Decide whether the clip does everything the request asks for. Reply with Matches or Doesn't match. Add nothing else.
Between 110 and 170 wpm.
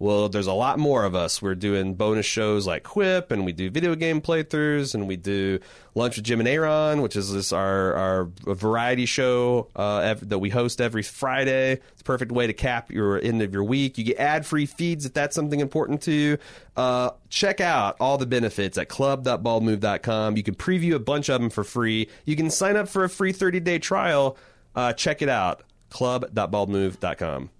Doesn't match